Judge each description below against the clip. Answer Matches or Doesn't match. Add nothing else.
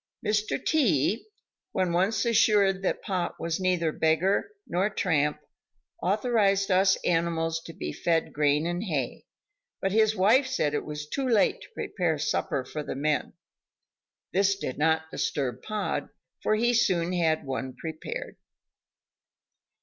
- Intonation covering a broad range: Doesn't match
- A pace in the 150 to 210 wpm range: Doesn't match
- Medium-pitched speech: Matches